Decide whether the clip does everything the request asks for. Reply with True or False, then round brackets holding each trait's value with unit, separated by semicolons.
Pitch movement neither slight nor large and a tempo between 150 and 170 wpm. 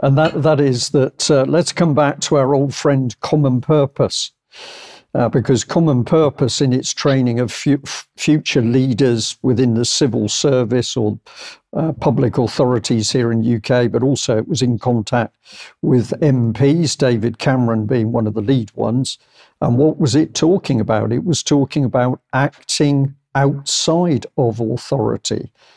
True (3.3 semitones; 155 wpm)